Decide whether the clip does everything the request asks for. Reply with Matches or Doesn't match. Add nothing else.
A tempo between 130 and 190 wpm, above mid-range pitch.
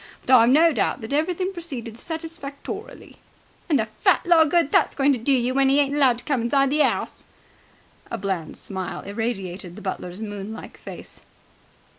Matches